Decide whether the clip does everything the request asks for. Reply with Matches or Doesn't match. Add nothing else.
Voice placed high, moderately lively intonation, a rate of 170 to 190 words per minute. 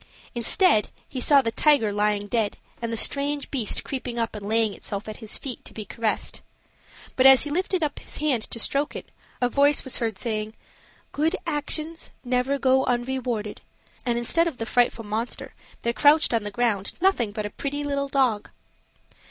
Matches